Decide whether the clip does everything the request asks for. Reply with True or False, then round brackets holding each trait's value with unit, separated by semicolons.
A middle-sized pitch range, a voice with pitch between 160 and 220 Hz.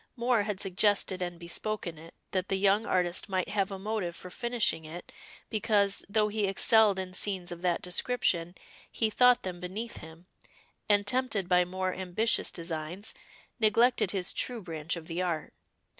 True (3.3 semitones; 190 Hz)